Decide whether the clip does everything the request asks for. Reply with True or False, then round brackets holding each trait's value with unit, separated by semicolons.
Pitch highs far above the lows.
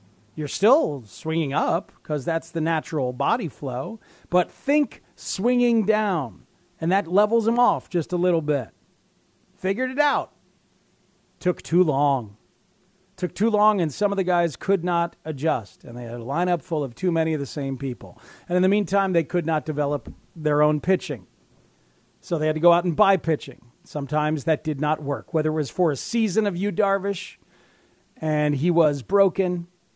False (4.4 semitones)